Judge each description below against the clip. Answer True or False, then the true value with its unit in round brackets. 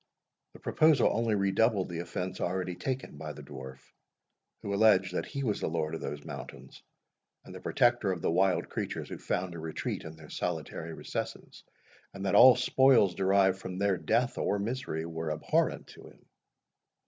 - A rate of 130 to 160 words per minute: False (175 wpm)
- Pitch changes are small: False (5.0 semitones)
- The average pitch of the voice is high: False (95 Hz)